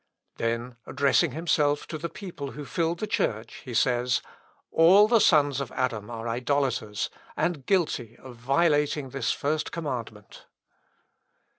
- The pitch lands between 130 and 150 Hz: Yes, medium, 140 Hz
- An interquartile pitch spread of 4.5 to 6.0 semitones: Yes, average, 5.1 semitones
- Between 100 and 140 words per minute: Yes, slow, 135 wpm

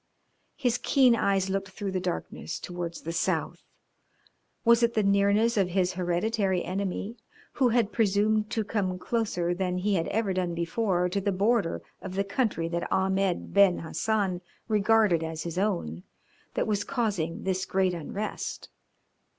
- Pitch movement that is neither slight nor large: Yes, average, 3.2 semitones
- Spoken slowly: No, average, 155 wpm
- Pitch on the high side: Yes, high, 195 Hz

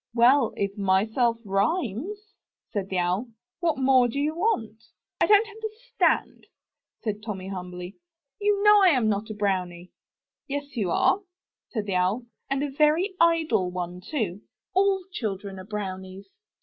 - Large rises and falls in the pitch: Yes, wide, 8.6 semitones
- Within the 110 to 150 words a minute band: Yes, average, 145 wpm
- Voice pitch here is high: Yes, high, 225 Hz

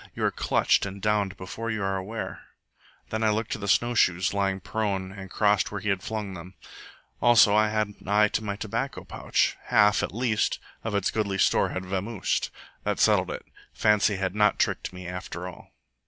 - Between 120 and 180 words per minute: No, average, 195 wpm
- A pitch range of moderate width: No, narrow, 2.1 semitones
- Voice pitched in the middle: No, low, 100 Hz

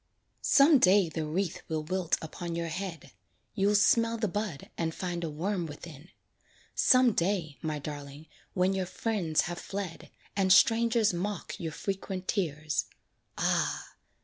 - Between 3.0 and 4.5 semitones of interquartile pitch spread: Yes, average, 4.2 semitones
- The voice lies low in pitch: No, medium, 180 Hz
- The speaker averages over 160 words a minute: No, average, 145 wpm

